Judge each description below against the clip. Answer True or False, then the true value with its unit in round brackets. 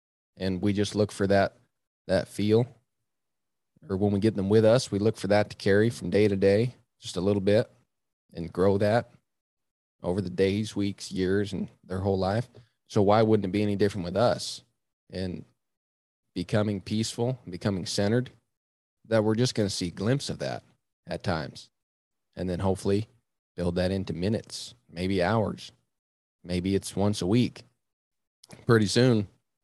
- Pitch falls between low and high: False (105 Hz)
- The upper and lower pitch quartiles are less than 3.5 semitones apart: True (2.9 semitones)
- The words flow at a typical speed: True (170 wpm)